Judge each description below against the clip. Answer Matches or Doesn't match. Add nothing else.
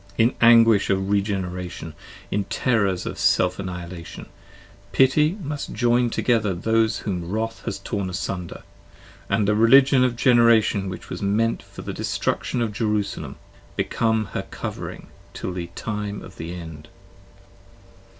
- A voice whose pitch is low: Matches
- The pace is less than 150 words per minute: Matches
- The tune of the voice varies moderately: Matches